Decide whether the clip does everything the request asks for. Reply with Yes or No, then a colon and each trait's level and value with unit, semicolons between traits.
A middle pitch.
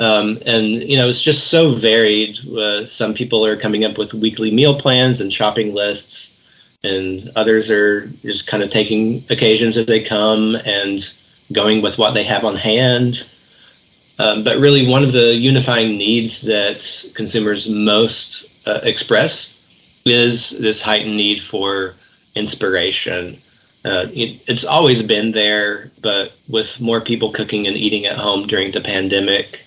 No: low, 110 Hz